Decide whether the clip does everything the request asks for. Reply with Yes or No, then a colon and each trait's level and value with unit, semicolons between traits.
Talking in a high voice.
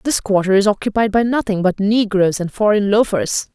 Yes: high, 205 Hz